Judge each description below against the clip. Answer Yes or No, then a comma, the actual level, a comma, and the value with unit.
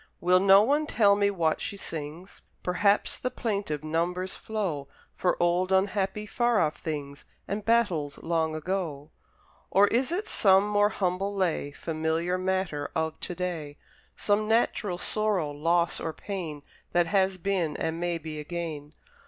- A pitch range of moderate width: Yes, average, 4.0 semitones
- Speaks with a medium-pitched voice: Yes, medium, 180 Hz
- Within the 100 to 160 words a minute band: Yes, average, 150 wpm